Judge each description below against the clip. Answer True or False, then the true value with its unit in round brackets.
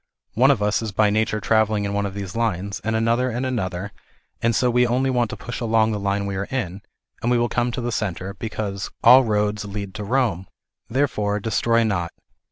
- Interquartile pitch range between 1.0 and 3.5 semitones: True (2.8 semitones)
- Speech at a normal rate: False (215 wpm)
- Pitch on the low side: True (110 Hz)